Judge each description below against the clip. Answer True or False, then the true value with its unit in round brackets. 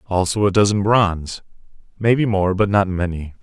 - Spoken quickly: False (160 wpm)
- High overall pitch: False (100 Hz)